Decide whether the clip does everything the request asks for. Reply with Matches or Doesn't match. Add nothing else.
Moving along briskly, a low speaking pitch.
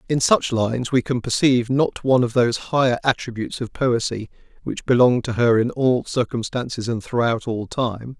Doesn't match